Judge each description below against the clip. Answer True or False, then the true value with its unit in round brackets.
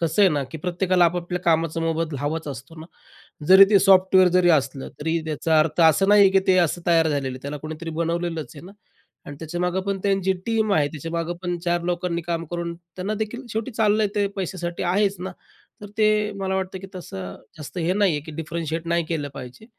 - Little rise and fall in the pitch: False (3.0 semitones)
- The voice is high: False (170 Hz)